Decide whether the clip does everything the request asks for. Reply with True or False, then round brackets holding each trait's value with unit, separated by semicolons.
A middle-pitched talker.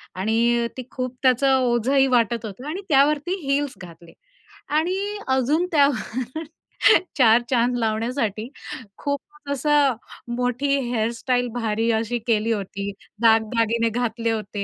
False (240 Hz)